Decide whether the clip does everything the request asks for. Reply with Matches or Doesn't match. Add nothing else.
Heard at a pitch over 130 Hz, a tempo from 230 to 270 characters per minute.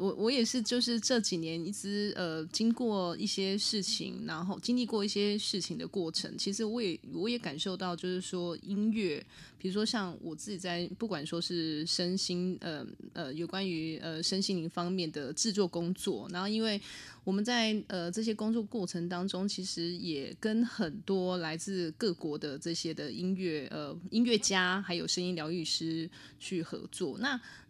Matches